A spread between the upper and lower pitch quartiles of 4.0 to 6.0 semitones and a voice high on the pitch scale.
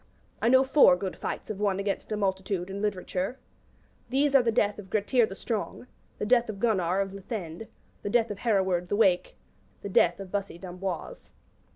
No: average, 2.8 semitones; high, 200 Hz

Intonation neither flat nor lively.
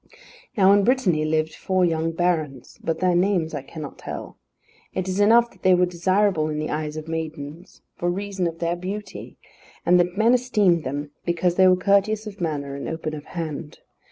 Yes: average, 3.6 semitones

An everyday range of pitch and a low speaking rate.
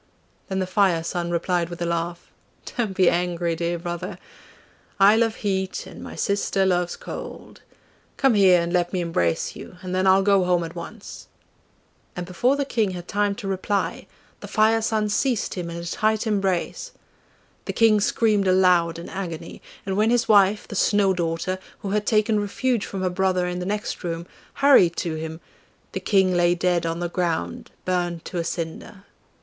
No: average, 3.0 semitones; average, 185 wpm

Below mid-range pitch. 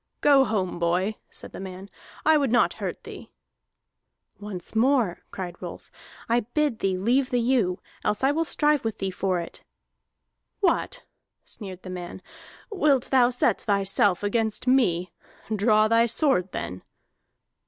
No: high, 215 Hz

